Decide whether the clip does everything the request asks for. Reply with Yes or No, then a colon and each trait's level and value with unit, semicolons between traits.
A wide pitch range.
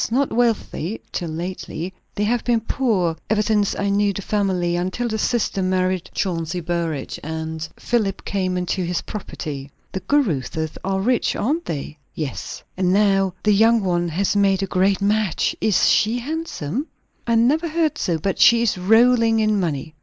No: average, 4.4 semitones